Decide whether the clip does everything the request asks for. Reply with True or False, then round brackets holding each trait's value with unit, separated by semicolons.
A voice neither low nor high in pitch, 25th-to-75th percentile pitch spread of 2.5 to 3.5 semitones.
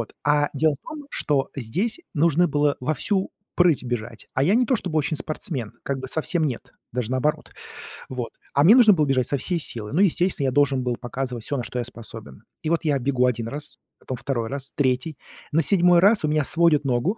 False (145 Hz; 4.8 semitones)